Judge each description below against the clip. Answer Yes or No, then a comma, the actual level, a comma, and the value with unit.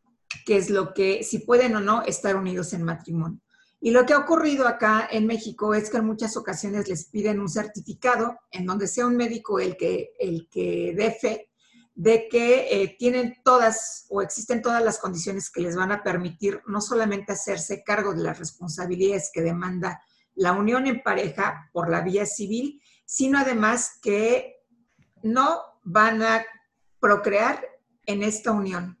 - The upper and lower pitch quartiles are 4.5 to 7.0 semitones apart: No, average, 3.6 semitones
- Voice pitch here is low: No, high, 215 Hz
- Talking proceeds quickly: No, average, 170 wpm